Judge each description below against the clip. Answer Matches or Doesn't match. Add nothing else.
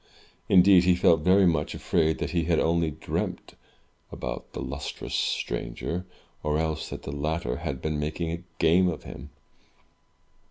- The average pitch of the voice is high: Doesn't match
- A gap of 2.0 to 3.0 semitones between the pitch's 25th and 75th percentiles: Matches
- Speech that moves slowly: Doesn't match